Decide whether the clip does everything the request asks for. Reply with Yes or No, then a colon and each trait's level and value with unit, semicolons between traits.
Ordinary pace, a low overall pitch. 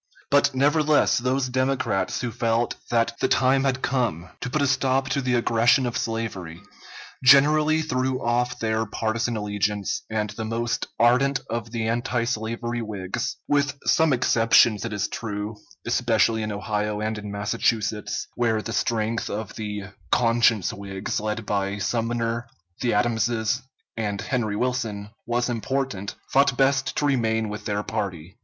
Yes: average, 150 wpm; low, 115 Hz